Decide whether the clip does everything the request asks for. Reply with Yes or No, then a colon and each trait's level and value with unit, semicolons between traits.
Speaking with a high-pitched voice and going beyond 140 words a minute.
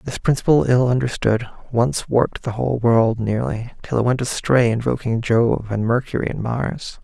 No: low, 120 Hz; average, 170 wpm